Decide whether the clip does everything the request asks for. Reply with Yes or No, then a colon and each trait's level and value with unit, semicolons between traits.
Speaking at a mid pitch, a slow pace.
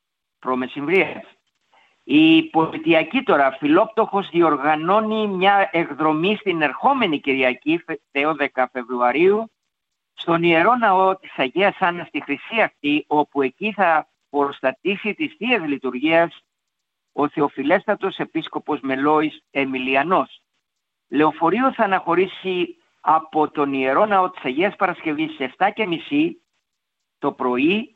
Yes: medium, 160 Hz; slow, 100 wpm